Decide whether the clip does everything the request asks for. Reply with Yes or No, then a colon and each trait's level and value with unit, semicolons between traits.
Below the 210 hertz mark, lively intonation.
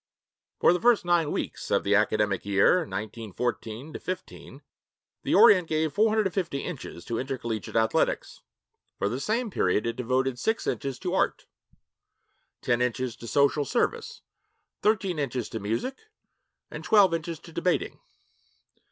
Yes: medium, 140 Hz; wide, 8.0 semitones